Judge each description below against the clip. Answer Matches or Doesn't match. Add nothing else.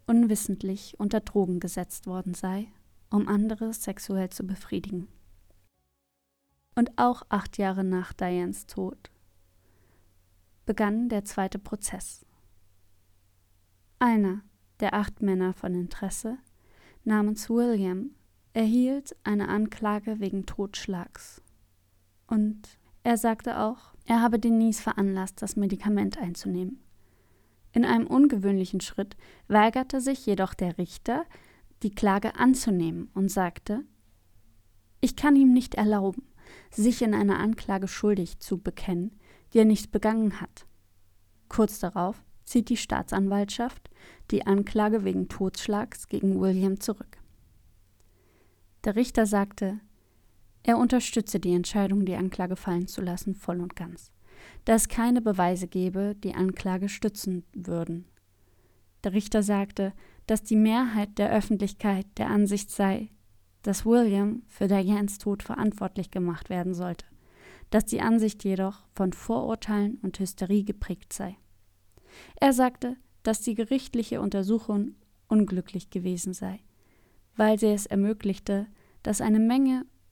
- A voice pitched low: Doesn't match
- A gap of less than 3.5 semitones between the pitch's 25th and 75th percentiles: Doesn't match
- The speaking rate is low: Matches